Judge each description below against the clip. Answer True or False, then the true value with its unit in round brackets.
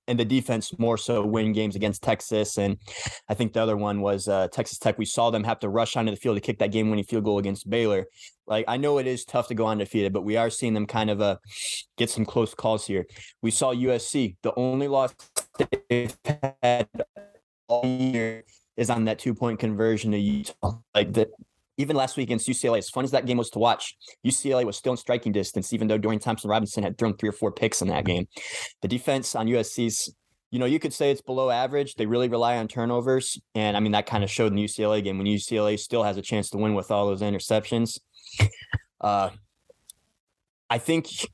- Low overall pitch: True (110 Hz)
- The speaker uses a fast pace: True (220 wpm)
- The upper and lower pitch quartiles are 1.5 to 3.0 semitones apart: True (2.7 semitones)